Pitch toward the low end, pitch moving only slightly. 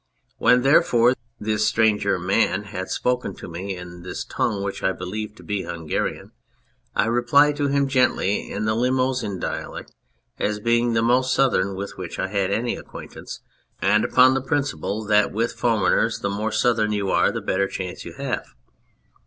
No: low, 110 Hz; average, 3.7 semitones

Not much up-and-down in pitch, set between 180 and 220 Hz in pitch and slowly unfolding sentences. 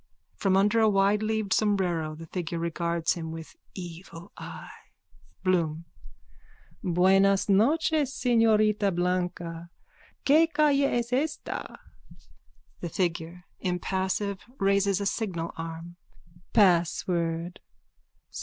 No: average, 3.9 semitones; high, 190 Hz; slow, 95 wpm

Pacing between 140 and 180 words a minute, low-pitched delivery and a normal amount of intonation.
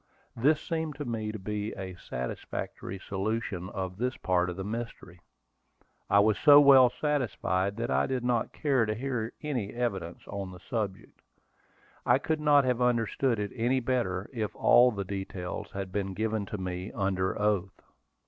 Yes: average, 165 wpm; low, 110 Hz; average, 4.5 semitones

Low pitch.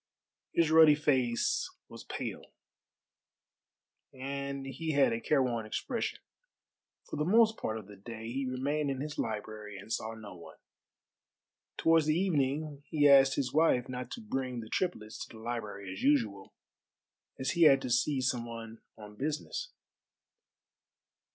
Yes: low, 130 Hz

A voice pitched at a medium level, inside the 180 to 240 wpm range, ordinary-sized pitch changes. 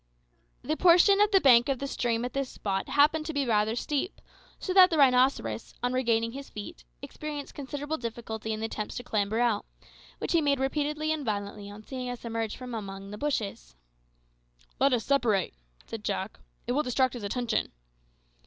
No: high, 245 Hz; average, 185 wpm; average, 4.7 semitones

